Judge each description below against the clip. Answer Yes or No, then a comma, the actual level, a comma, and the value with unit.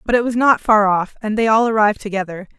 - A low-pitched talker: No, high, 215 Hz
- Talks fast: Yes, fast, 255 wpm